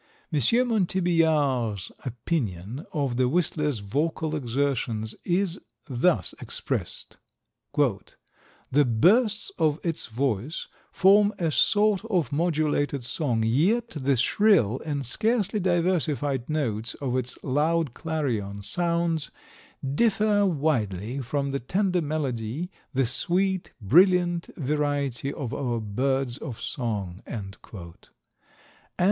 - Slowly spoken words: Yes, slow, 105 wpm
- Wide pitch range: Yes, wide, 6.2 semitones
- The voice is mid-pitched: Yes, medium, 145 Hz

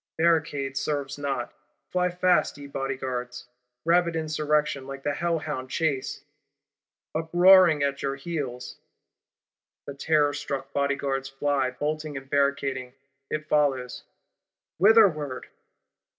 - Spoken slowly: Yes, slow, 100 wpm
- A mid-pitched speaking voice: Yes, medium, 145 Hz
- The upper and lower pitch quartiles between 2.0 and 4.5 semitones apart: Yes, narrow, 2.6 semitones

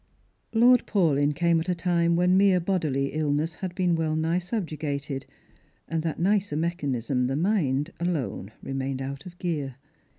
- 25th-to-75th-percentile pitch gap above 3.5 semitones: Yes, average, 4.0 semitones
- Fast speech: No, average, 155 wpm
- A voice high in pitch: No, medium, 165 Hz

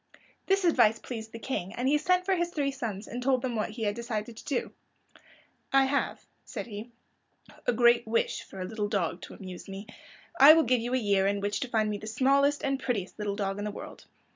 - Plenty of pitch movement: No, average, 4.6 semitones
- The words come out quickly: Yes, fast, 230 wpm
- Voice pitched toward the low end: No, high, 235 Hz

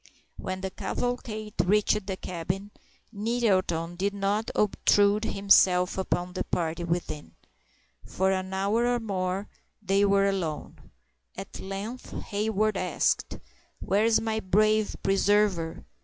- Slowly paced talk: Yes, slow, 120 wpm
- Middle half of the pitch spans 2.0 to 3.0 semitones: Yes, narrow, 2.4 semitones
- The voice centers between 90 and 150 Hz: No, high, 195 Hz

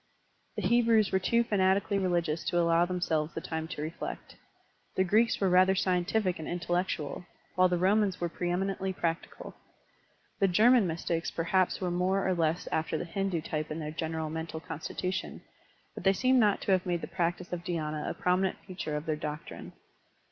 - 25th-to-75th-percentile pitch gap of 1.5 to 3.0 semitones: Yes, average, 2.7 semitones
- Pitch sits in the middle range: Yes, medium, 180 Hz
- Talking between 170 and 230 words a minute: Yes, average, 185 wpm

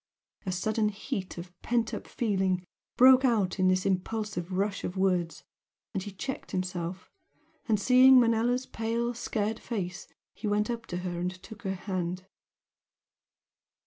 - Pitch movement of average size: Yes, average, 3.7 semitones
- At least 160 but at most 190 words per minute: No, average, 145 wpm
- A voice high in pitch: Yes, high, 200 Hz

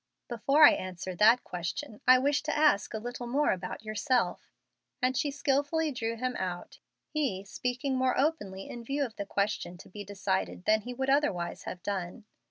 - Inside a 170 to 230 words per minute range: Yes, average, 180 wpm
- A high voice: Yes, high, 240 Hz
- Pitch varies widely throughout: Yes, wide, 5.9 semitones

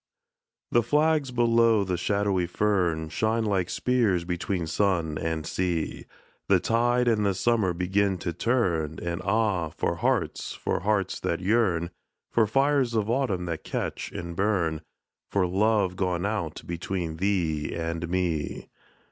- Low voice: Yes, very low, 95 Hz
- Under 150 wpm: Yes, average, 140 wpm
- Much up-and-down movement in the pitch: No, average, 4.4 semitones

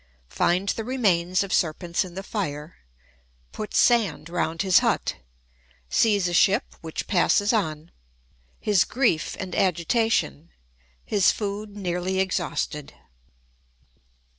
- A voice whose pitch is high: No, medium, 175 Hz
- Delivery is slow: Yes, slow, 95 wpm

